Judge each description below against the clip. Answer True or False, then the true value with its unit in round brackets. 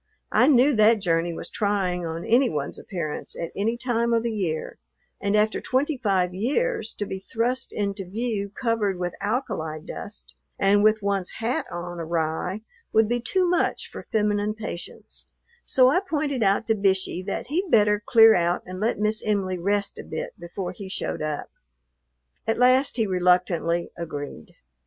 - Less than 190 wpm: True (170 wpm)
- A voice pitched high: True (205 Hz)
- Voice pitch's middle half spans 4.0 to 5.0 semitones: True (4.4 semitones)